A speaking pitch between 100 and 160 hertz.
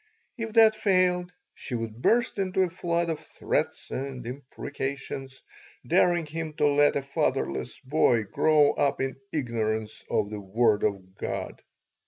Yes: medium, 140 Hz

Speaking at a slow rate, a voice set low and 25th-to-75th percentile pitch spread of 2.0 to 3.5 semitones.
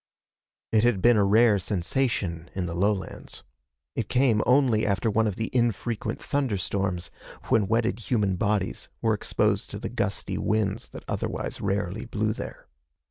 No: average, 150 wpm; low, 105 Hz; average, 2.9 semitones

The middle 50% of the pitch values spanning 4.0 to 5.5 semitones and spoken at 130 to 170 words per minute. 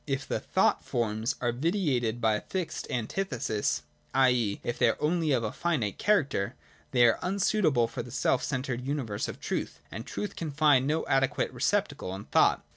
No: average, 5.2 semitones; average, 180 wpm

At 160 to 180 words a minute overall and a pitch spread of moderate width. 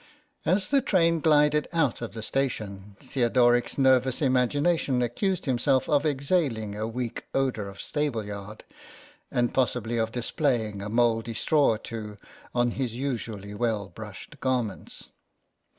No: slow, 135 wpm; average, 4.2 semitones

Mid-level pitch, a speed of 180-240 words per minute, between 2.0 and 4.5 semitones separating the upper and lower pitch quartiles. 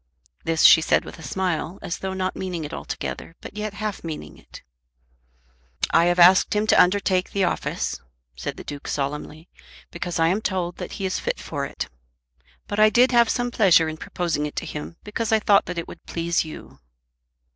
Yes: medium, 180 Hz; average, 200 wpm; average, 3.8 semitones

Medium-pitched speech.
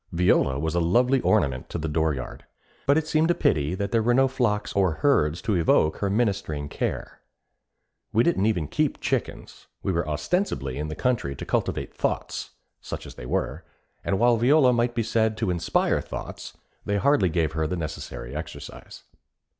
No: very low, 95 Hz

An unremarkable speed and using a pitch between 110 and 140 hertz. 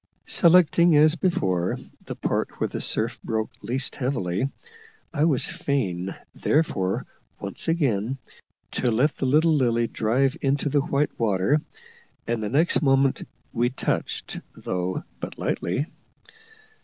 No: slow, 130 wpm; low, 135 Hz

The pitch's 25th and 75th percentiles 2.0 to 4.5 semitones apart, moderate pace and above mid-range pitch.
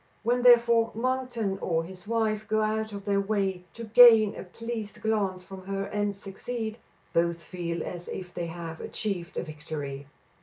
Yes: average, 3.9 semitones; average, 165 wpm; high, 200 Hz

